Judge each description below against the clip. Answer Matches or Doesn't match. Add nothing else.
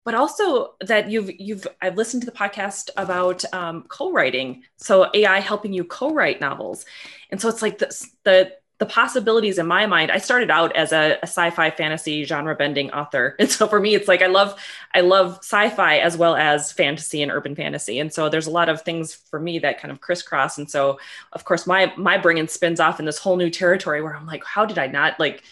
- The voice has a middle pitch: Matches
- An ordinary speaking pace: Doesn't match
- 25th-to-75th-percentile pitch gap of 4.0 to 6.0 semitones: Matches